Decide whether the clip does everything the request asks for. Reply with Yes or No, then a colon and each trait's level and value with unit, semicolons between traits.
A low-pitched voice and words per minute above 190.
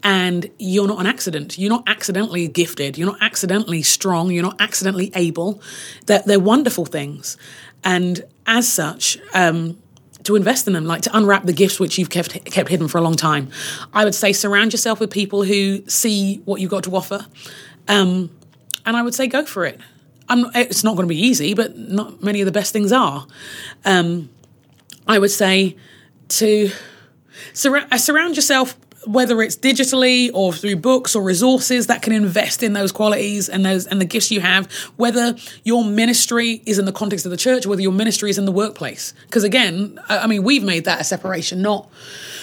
No: high, 200 Hz; average, 200 wpm